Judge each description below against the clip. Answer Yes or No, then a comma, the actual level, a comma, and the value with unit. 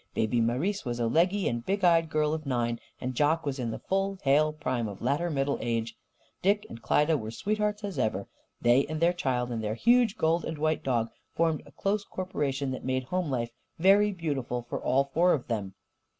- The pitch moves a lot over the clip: Yes, wide, 6.5 semitones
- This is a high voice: No, medium, 145 Hz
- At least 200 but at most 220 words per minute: Yes, fast, 205 wpm